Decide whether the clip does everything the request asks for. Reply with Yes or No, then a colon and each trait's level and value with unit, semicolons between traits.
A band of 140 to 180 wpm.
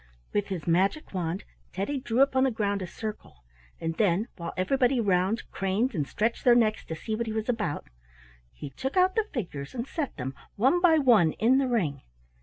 No: average, 200 wpm